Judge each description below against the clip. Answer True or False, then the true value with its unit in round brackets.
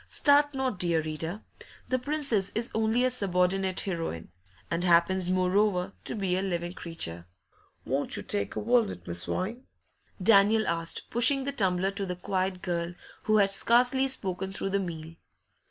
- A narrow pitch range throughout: False (4.2 semitones)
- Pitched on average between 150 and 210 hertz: True (190 Hz)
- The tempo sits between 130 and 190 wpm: True (160 wpm)